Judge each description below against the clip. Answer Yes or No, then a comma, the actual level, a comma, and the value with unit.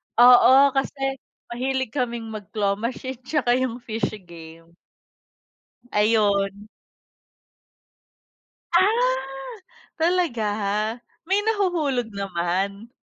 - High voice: Yes, high, 235 Hz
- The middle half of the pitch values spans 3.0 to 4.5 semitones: No, average, 5.1 semitones